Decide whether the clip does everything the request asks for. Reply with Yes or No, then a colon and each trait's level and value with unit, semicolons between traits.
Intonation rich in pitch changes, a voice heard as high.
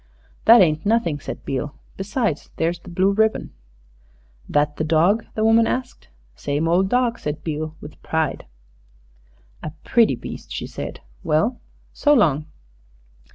No: wide, 6.5 semitones; medium, 170 Hz